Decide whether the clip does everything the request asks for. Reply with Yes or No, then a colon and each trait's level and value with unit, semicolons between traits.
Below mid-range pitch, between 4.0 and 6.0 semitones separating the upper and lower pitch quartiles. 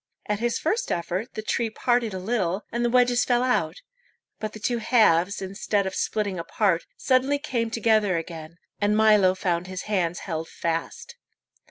No: high, 210 Hz; average, 4.6 semitones